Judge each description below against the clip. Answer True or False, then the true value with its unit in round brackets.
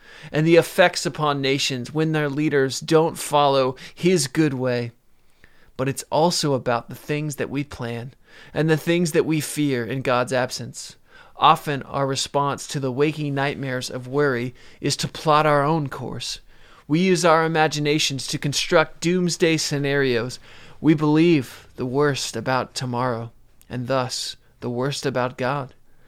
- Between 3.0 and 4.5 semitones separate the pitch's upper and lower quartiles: True (3.6 semitones)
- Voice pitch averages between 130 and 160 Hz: True (140 Hz)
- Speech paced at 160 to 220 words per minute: False (150 wpm)